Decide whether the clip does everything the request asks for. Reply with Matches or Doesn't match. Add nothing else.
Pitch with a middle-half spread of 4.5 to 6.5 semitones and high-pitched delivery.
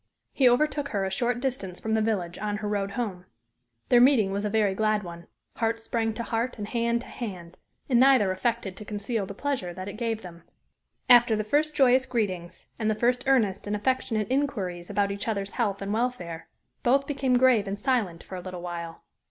Doesn't match